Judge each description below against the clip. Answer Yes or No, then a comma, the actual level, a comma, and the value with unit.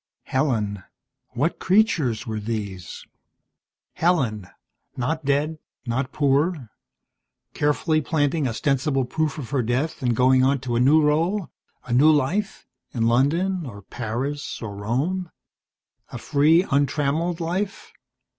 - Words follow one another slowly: Yes, slow, 120 wpm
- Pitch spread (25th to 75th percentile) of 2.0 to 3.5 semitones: No, average, 4.7 semitones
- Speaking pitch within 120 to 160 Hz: Yes, medium, 140 Hz